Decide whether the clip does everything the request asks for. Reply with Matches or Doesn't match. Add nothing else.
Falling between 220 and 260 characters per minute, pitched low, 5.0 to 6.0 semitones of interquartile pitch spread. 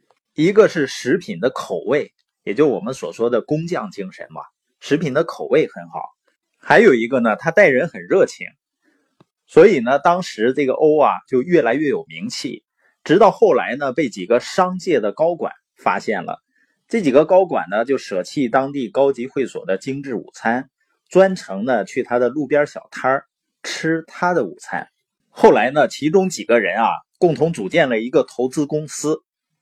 Doesn't match